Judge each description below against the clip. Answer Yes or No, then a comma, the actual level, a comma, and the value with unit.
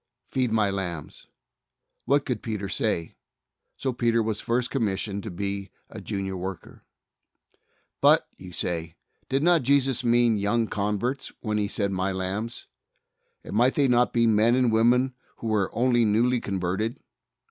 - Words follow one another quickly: No, average, 150 wpm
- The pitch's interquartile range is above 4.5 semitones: No, average, 3.7 semitones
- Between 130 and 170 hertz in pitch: No, low, 110 Hz